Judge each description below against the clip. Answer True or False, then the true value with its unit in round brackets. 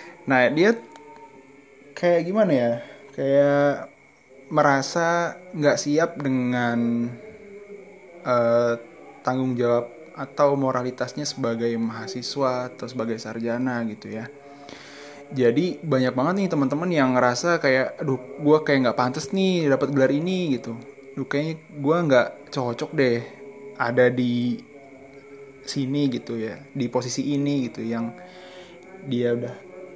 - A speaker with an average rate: True (115 wpm)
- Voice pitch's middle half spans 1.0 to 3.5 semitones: True (3.1 semitones)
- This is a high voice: False (135 Hz)